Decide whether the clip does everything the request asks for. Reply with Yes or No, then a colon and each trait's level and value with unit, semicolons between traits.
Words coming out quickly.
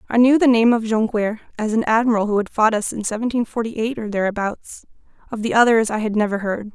Yes: fast, 230 wpm